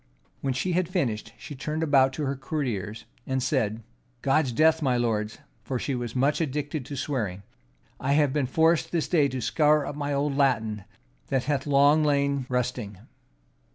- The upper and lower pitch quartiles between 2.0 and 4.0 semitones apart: Yes, average, 3.1 semitones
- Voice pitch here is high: No, medium, 140 Hz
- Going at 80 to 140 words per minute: No, average, 175 wpm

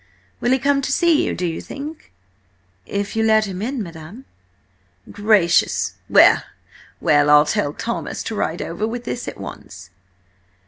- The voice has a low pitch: No, high, 210 Hz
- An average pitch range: No, wide, 6.8 semitones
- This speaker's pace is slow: No, average, 155 wpm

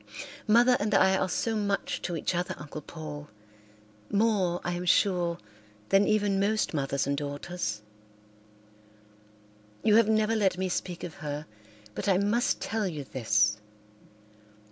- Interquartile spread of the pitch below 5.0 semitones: No, wide, 5.6 semitones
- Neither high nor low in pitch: Yes, medium, 180 Hz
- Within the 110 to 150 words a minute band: Yes, average, 145 wpm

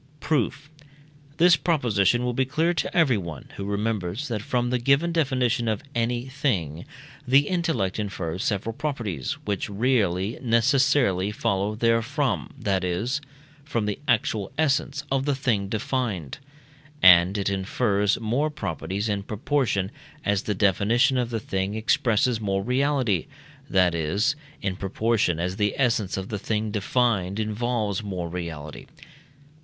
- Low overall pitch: Yes, low, 110 Hz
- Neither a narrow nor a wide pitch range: Yes, average, 5.0 semitones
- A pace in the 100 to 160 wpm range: Yes, average, 140 wpm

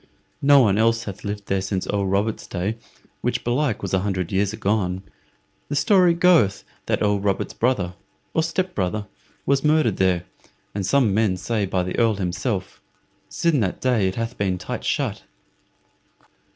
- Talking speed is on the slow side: No, average, 165 wpm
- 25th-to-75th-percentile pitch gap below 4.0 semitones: No, average, 4.6 semitones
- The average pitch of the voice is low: Yes, low, 105 Hz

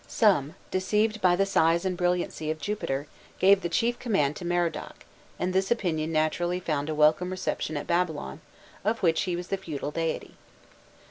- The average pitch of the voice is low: No, medium, 175 Hz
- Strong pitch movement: No, average, 3.3 semitones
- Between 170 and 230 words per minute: Yes, average, 175 wpm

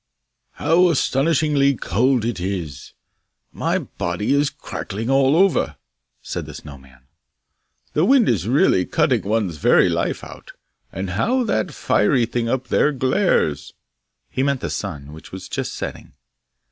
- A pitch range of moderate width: No, wide, 7.9 semitones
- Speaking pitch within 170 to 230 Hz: No, low, 125 Hz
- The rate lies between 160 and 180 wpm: No, average, 145 wpm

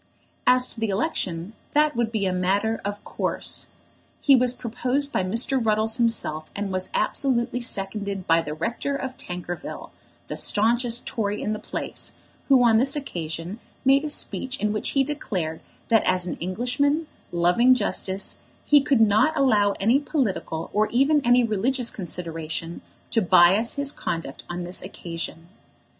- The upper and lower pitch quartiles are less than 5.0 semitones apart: No, wide, 5.6 semitones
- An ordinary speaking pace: Yes, average, 155 wpm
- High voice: Yes, high, 220 Hz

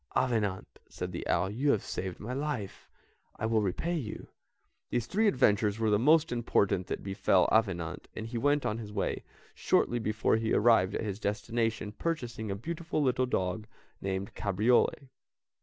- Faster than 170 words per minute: No, average, 165 wpm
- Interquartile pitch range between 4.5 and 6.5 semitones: No, average, 3.8 semitones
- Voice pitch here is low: Yes, low, 110 Hz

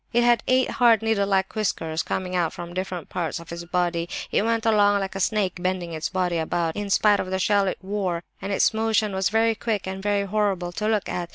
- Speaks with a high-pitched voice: Yes, high, 195 Hz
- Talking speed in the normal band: No, fast, 235 wpm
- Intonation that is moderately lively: Yes, average, 3.2 semitones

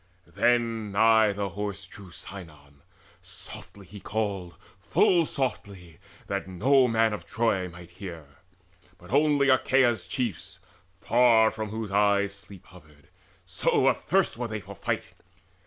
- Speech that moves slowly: Yes, slow, 130 wpm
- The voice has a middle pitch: No, low, 105 Hz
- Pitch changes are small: No, average, 3.6 semitones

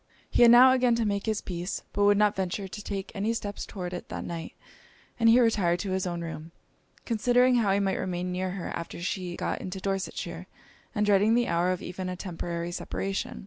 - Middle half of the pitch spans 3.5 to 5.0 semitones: No, average, 3.1 semitones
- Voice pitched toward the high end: Yes, high, 195 Hz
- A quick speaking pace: Yes, fast, 215 wpm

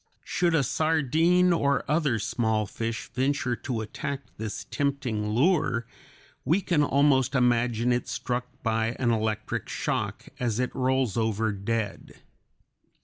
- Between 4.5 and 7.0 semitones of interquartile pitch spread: No, average, 4.0 semitones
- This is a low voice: Yes, low, 125 Hz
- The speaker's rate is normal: No, slow, 130 wpm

